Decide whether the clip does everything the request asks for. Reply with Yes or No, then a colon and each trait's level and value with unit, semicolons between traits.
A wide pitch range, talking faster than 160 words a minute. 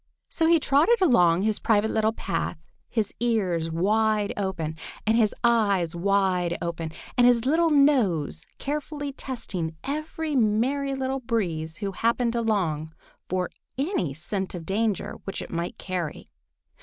No: wide, 6.7 semitones; average, 140 wpm